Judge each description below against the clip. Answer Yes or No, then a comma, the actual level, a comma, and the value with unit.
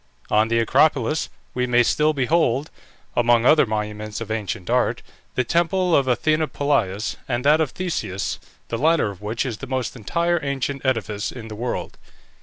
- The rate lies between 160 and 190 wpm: Yes, average, 170 wpm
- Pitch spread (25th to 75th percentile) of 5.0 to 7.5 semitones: Yes, wide, 5.4 semitones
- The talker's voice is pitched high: No, low, 125 Hz